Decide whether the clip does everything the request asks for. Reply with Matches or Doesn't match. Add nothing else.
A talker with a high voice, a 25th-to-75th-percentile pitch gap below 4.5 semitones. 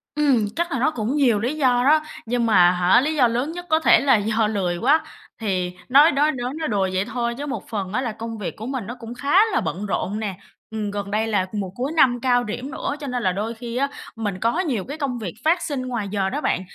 Doesn't match